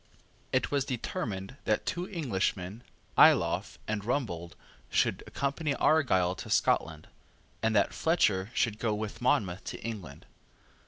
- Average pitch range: No, wide, 5.8 semitones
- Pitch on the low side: Yes, low, 110 Hz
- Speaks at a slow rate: Yes, slow, 125 wpm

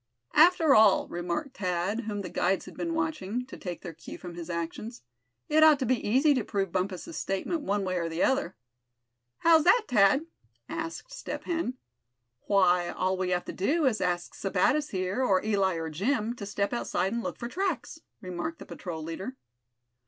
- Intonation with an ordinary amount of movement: No, wide, 7.4 semitones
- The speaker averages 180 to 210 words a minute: Yes, average, 190 wpm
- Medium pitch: No, high, 205 Hz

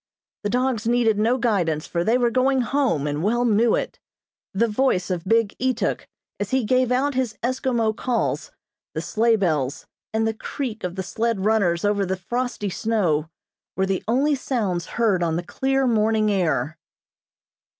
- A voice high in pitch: Yes, high, 220 Hz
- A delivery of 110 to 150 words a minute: No, average, 170 wpm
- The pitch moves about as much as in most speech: Yes, average, 4.6 semitones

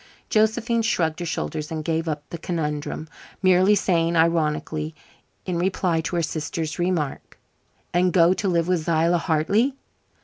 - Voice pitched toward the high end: No, medium, 170 Hz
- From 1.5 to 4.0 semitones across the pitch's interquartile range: Yes, narrow, 2.6 semitones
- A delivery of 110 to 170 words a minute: Yes, average, 145 wpm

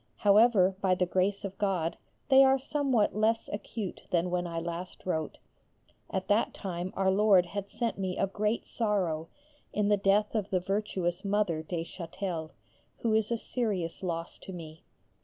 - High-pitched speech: Yes, high, 195 Hz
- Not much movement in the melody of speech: No, average, 3.1 semitones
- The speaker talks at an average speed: Yes, average, 170 wpm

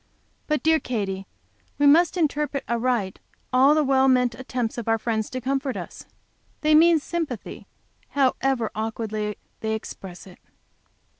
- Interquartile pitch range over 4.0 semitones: Yes, average, 4.5 semitones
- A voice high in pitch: Yes, very high, 255 Hz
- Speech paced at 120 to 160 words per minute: Yes, average, 140 wpm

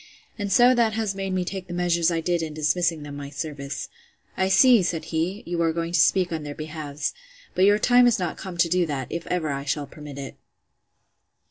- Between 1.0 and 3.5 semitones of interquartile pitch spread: No, average, 3.9 semitones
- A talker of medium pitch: Yes, medium, 170 Hz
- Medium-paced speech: No, fast, 220 wpm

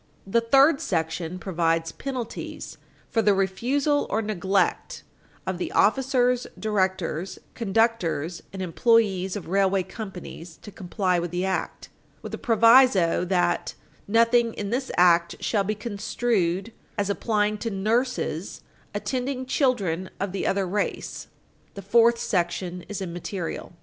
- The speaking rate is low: Yes, slow, 130 wpm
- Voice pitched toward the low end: No, high, 200 Hz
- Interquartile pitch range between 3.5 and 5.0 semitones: Yes, average, 4.2 semitones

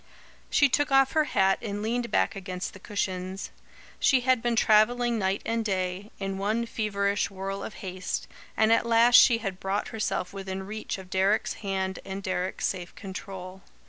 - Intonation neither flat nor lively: Yes, average, 3.2 semitones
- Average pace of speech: Yes, average, 175 wpm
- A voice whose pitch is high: Yes, high, 200 Hz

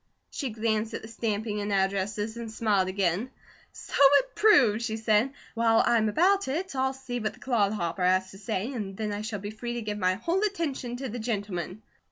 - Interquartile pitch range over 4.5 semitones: No, average, 3.1 semitones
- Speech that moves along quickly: Yes, fast, 215 wpm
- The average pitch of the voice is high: Yes, high, 220 Hz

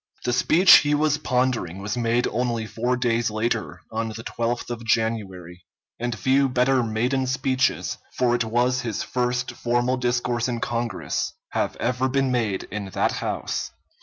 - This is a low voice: Yes, low, 120 Hz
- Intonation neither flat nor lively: No, narrow, 1.9 semitones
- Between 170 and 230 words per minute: No, average, 160 wpm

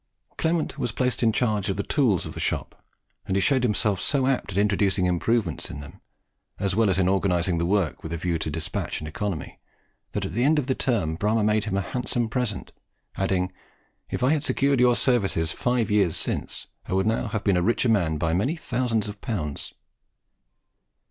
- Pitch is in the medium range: No, low, 105 Hz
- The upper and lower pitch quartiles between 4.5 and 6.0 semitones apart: Yes, average, 5.1 semitones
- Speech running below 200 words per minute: No, fast, 205 wpm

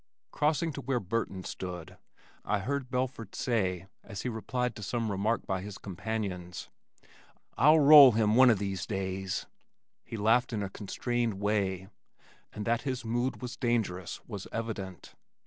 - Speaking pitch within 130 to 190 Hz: No, low, 110 Hz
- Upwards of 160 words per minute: No, average, 150 wpm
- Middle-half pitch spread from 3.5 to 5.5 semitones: Yes, average, 4.2 semitones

